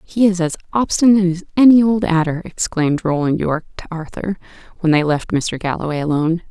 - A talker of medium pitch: Yes, medium, 175 Hz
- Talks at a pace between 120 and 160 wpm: No, average, 175 wpm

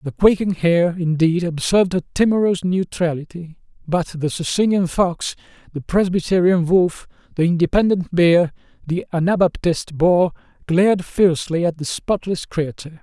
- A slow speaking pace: Yes, slow, 125 wpm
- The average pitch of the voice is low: No, medium, 175 Hz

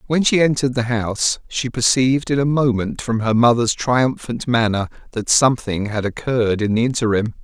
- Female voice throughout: No, male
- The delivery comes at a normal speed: Yes, average, 180 wpm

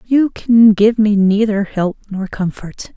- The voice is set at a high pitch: Yes, high, 210 Hz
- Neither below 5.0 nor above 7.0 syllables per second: No, 3.7 syllables/s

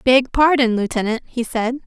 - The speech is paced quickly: No, average, 160 wpm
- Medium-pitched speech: No, high, 245 Hz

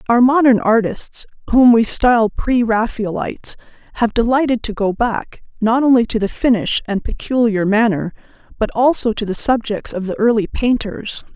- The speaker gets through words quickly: No, average, 160 wpm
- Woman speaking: Yes, female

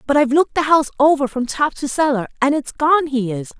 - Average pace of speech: No, fast, 250 wpm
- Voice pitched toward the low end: No, very high, 280 Hz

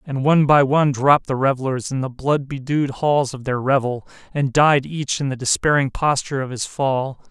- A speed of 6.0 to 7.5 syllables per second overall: No, 5.4 syllables/s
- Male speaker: Yes, male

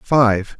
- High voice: No, low, 115 Hz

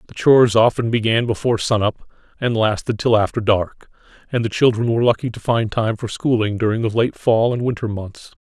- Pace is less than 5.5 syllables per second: No, 5.6 syllables/s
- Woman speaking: No, male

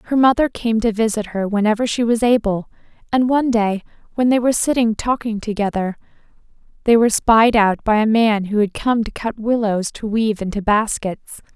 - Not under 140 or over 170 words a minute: No, average, 185 wpm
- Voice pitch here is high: Yes, high, 220 Hz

